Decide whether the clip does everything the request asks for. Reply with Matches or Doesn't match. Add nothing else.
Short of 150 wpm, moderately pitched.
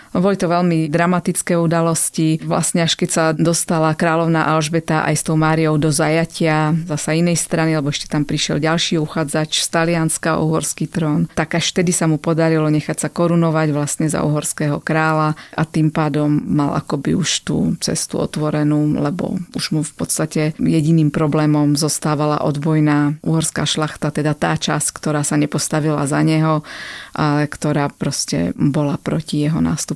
Doesn't match